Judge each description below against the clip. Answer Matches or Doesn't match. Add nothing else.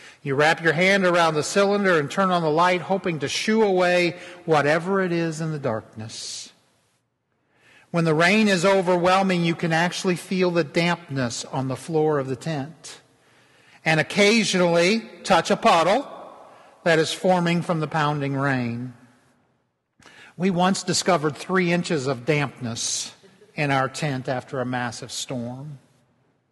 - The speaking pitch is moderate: Matches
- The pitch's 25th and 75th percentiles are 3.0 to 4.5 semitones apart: Doesn't match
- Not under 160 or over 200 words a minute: Doesn't match